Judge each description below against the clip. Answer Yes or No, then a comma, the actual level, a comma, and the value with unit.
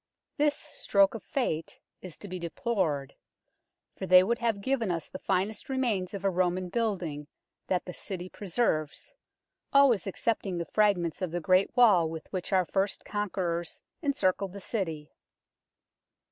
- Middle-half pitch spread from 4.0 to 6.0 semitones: No, average, 3.6 semitones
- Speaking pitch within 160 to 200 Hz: Yes, high, 190 Hz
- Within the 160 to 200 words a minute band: No, average, 150 wpm